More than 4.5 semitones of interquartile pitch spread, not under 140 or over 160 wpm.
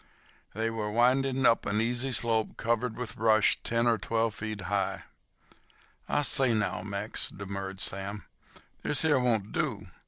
No: average, 2.9 semitones; average, 150 wpm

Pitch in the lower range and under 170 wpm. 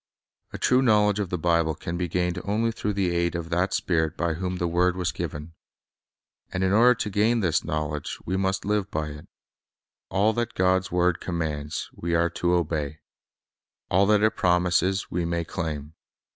No: very low, 90 Hz; average, 185 wpm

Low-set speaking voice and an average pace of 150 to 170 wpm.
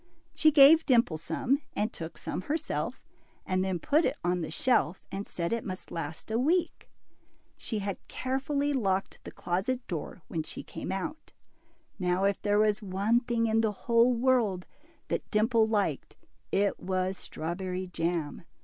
No: high, 205 Hz; average, 160 wpm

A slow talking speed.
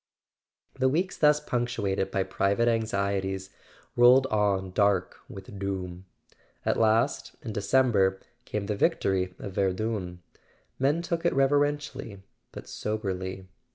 Yes: slow, 120 wpm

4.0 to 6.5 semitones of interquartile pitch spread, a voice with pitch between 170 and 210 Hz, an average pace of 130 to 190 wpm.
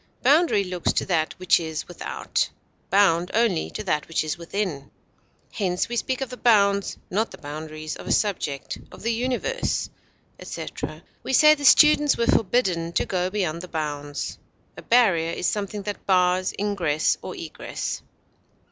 Yes: wide, 5.6 semitones; medium, 185 Hz; average, 160 wpm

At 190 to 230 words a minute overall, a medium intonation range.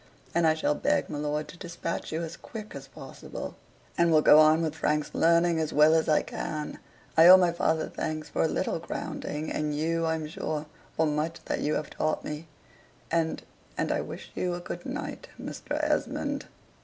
No: average, 195 wpm; narrow, 1.7 semitones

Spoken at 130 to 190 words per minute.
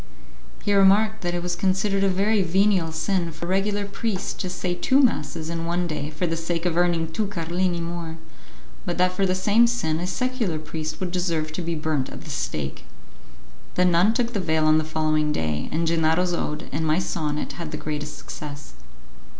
No: average, 200 wpm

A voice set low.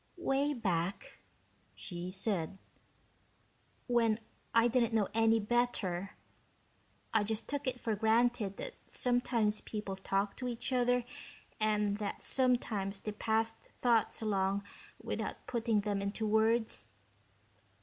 No: high, 220 Hz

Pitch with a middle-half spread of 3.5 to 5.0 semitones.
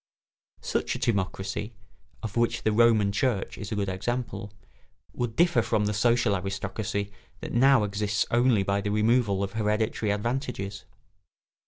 No: average, 2.8 semitones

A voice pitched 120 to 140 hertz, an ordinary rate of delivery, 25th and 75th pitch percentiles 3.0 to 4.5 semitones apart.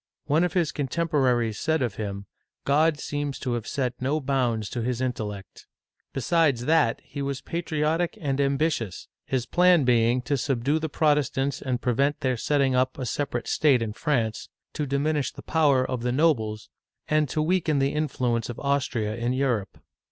Yes: low, 135 Hz; average, 170 wpm; average, 3.8 semitones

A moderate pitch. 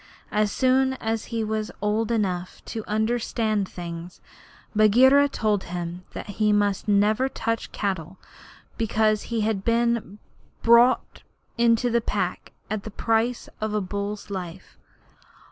No: high, 215 Hz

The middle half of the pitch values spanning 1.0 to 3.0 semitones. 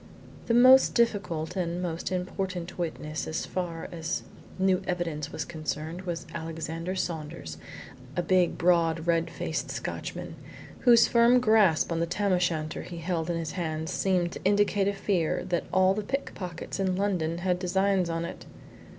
Yes: narrow, 2.6 semitones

